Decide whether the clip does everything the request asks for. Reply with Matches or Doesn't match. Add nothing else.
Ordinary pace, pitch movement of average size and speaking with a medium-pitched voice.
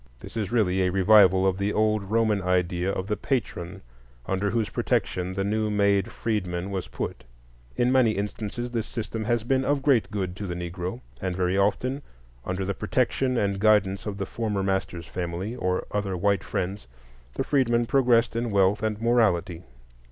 Doesn't match